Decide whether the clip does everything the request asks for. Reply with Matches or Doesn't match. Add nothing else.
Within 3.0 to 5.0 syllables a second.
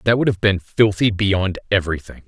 Doesn't match